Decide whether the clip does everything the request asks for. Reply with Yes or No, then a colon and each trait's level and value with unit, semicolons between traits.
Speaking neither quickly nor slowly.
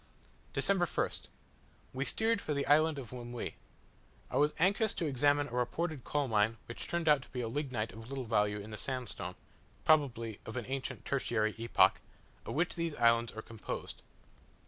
Yes: average, 170 wpm